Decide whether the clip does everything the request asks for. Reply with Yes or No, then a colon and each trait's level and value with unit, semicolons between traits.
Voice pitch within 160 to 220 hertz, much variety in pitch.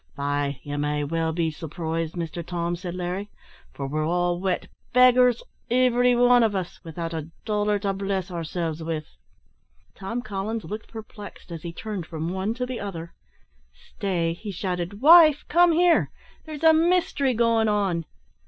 Yes: high, 190 Hz; wide, 5.7 semitones